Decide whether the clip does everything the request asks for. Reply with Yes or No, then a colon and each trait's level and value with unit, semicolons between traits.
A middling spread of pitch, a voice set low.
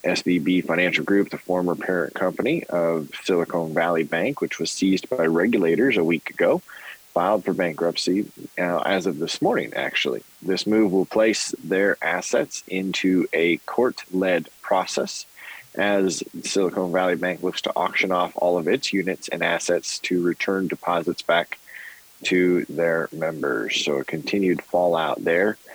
No: narrow, 1.9 semitones; very low, 90 Hz